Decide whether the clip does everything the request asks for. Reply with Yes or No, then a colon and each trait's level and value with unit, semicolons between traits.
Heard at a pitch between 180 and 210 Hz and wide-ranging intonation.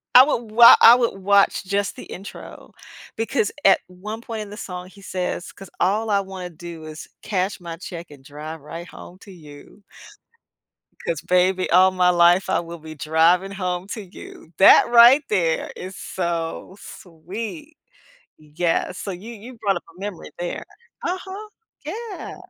No: medium, 185 Hz; average, 3.7 semitones